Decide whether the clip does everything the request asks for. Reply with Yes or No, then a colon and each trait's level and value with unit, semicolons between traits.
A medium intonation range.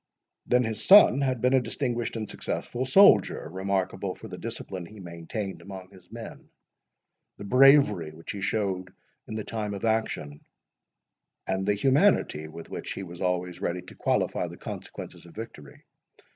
Yes: average, 4.7 semitones